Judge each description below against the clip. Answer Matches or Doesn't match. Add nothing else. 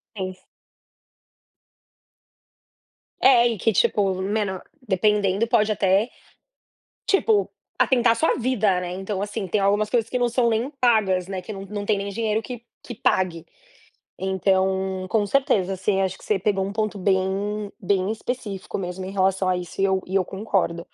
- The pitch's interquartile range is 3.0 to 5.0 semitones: Doesn't match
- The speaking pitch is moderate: Doesn't match